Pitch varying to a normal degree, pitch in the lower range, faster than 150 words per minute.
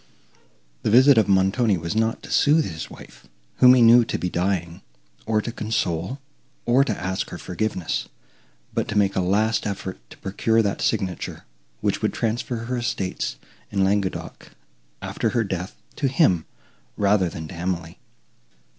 Yes: average, 3.7 semitones; low, 100 Hz; average, 160 wpm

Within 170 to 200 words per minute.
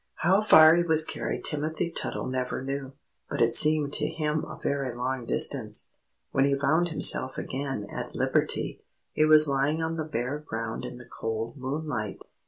Yes: average, 175 wpm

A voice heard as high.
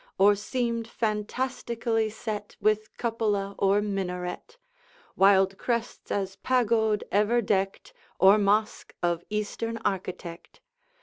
Yes: high, 210 Hz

